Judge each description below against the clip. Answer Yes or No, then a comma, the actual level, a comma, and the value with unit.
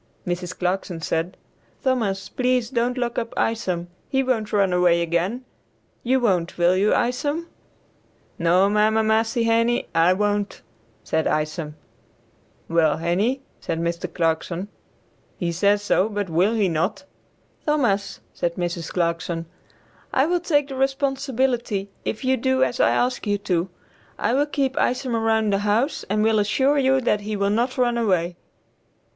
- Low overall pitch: No, high, 210 Hz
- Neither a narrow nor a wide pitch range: No, wide, 5.8 semitones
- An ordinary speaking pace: Yes, average, 150 wpm